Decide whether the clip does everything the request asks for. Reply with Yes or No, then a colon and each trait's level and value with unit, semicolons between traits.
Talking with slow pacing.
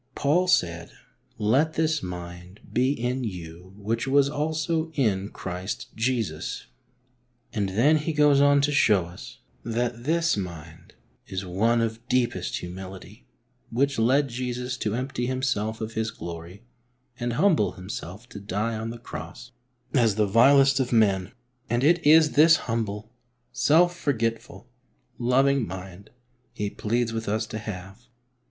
No: average, 145 wpm